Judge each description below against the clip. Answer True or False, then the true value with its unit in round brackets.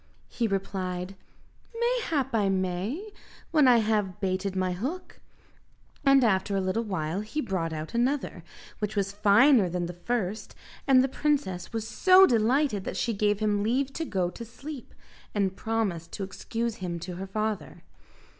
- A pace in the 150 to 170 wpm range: True (160 wpm)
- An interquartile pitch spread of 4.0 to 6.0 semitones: True (5.0 semitones)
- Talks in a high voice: True (210 Hz)